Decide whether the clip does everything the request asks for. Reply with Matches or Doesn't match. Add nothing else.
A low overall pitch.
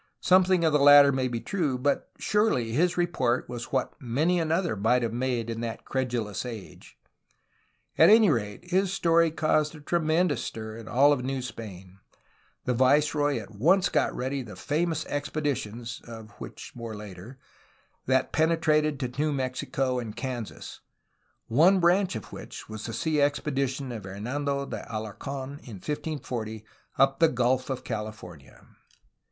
Matches